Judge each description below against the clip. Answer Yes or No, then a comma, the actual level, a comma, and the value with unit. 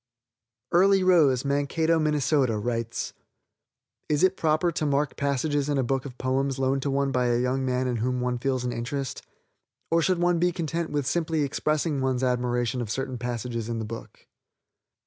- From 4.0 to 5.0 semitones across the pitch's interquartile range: No, average, 3.5 semitones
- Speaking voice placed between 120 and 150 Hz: Yes, low, 135 Hz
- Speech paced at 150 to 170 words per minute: No, average, 180 wpm